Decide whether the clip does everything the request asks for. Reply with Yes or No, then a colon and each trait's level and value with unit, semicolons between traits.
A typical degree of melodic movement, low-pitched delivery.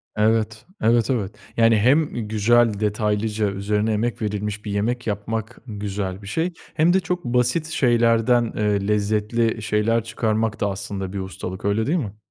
No: narrow, 2.3 semitones; low, 110 Hz